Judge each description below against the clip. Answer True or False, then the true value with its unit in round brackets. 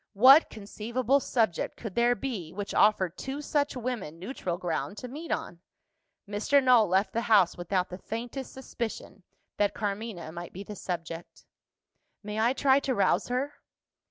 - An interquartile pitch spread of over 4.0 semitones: True (5.2 semitones)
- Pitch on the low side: False (215 Hz)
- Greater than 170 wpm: False (155 wpm)